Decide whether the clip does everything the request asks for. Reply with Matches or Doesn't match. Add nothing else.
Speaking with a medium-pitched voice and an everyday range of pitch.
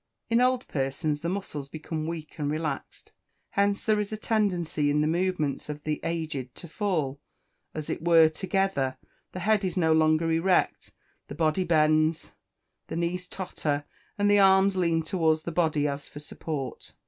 Matches